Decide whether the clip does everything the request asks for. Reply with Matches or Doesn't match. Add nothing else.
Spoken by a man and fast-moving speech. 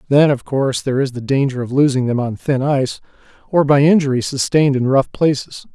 Matches